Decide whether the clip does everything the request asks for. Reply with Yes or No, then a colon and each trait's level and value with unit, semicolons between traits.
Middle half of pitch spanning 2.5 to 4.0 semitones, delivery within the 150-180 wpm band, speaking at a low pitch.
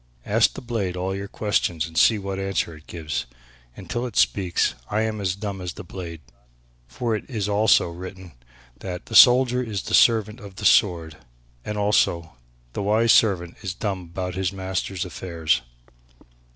Yes: average, 3.2 semitones; average, 170 wpm; very low, 95 Hz